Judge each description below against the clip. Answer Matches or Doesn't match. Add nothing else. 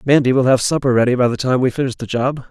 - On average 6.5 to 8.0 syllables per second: Matches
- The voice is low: Matches